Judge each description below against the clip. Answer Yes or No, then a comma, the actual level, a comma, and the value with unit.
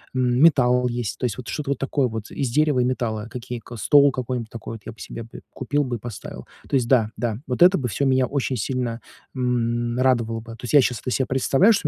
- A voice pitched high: No, low, 125 Hz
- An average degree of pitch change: No, narrow, 2.2 semitones